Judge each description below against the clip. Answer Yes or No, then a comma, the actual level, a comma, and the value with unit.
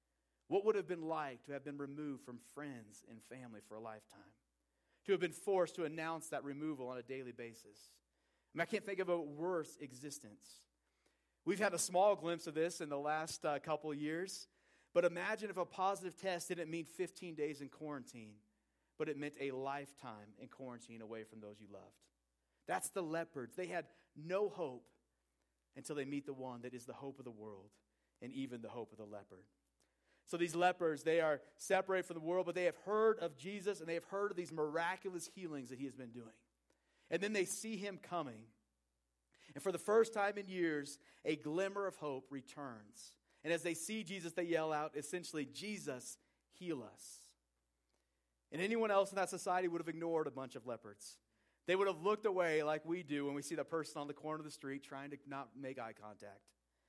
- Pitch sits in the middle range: Yes, medium, 150 Hz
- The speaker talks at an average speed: No, fast, 210 wpm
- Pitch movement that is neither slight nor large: No, wide, 6.3 semitones